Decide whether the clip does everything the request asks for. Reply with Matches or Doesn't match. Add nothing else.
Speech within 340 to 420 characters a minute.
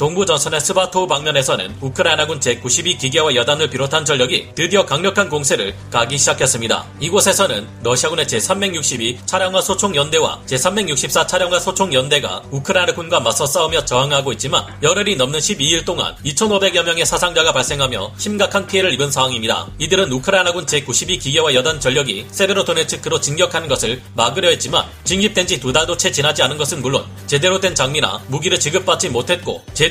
Matches